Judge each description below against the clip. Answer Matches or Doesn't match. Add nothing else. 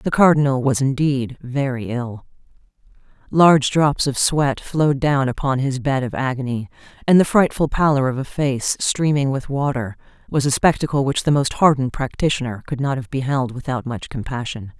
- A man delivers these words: Doesn't match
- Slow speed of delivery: Doesn't match